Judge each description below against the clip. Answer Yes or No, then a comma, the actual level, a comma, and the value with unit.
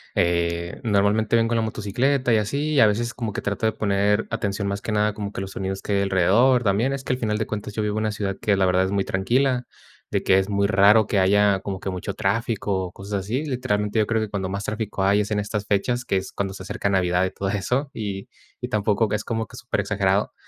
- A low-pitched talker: Yes, low, 105 Hz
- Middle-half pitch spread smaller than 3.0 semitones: Yes, narrow, 2.4 semitones